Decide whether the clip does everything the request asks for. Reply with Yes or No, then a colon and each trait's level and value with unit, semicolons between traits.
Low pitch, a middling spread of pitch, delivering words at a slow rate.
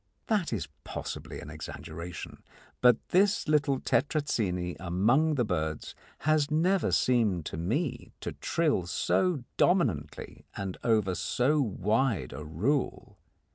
No: low, 120 Hz; wide, 9.0 semitones; slow, 120 wpm